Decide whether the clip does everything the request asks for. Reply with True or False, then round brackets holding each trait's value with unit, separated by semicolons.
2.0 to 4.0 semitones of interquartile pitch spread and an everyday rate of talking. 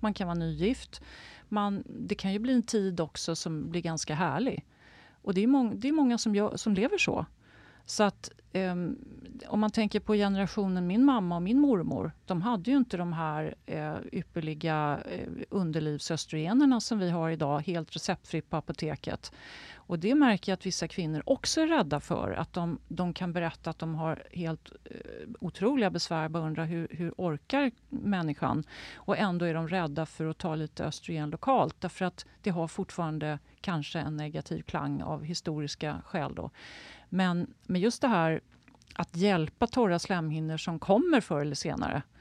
False (4.6 semitones; 175 wpm)